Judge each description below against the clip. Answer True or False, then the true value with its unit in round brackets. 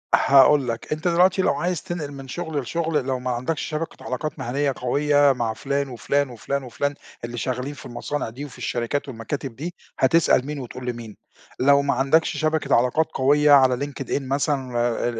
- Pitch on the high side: False (140 Hz)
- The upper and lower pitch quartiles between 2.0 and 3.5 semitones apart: True (2.8 semitones)